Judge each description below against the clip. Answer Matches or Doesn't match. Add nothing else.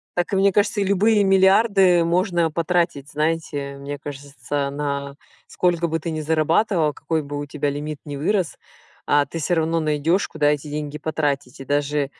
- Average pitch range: Matches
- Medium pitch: Matches